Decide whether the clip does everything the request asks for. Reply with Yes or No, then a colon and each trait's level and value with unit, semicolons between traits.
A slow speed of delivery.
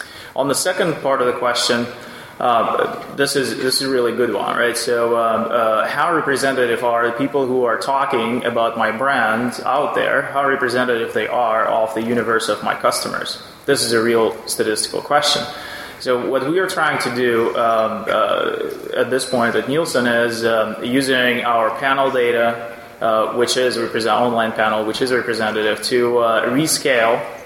No: average, 175 wpm